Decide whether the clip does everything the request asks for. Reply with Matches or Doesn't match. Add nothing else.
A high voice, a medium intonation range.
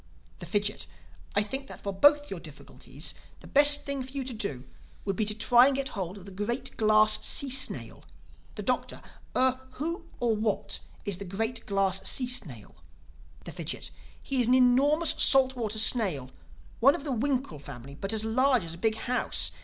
Matches